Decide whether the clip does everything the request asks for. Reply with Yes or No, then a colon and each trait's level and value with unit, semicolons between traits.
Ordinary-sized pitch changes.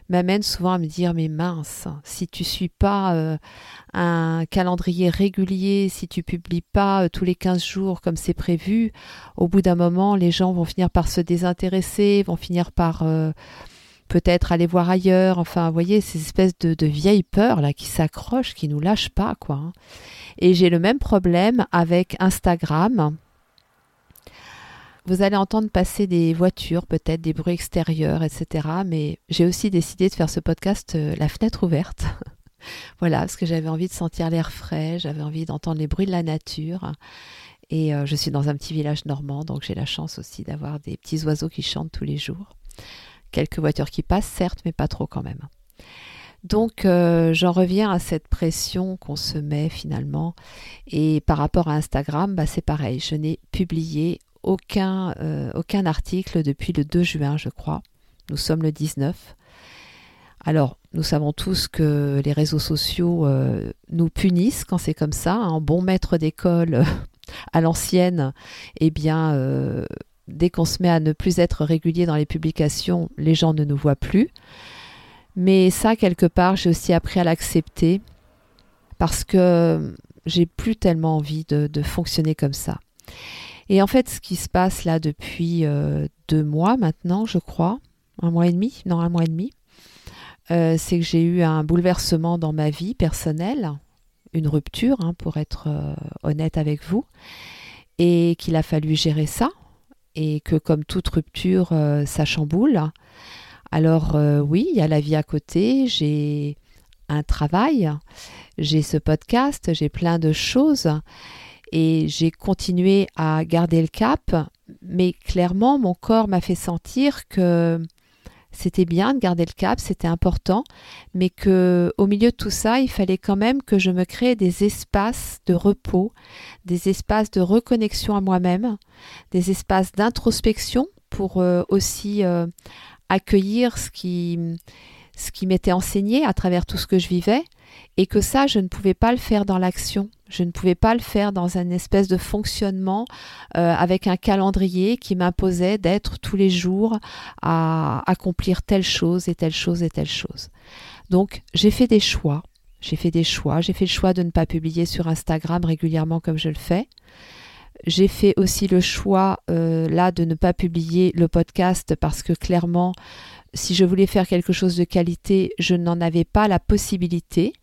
Yes: average, 3.0 semitones